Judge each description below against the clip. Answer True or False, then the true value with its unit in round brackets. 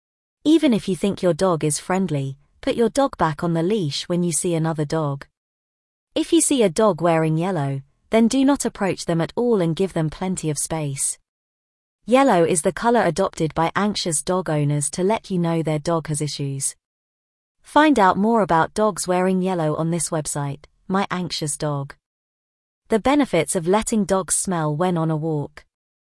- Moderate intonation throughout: True (4.5 semitones)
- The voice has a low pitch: False (170 Hz)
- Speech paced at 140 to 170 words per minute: False (185 wpm)